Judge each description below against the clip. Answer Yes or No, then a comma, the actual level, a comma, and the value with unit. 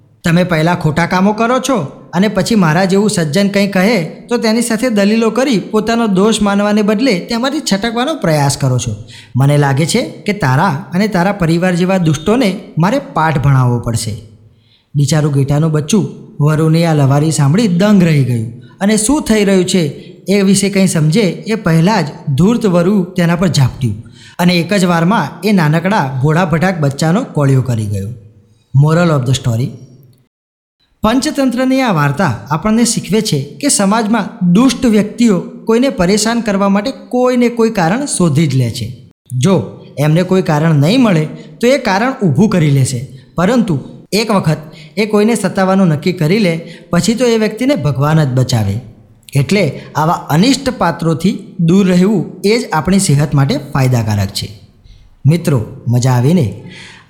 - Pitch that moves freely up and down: Yes, wide, 6.7 semitones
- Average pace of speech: No, fast, 155 wpm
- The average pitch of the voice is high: No, medium, 175 Hz